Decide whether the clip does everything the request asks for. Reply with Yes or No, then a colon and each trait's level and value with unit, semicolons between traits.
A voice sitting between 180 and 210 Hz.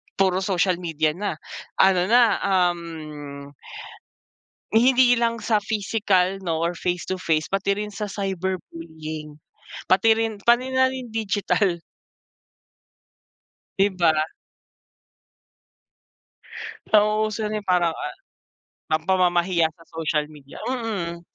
Yes: high, 190 Hz